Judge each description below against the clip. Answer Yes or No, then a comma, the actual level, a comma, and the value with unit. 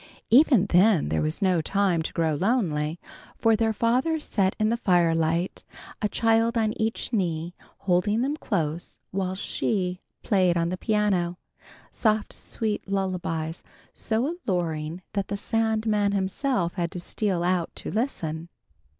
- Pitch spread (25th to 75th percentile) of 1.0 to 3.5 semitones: No, average, 4.3 semitones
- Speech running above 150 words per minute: No, average, 140 wpm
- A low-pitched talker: No, high, 195 Hz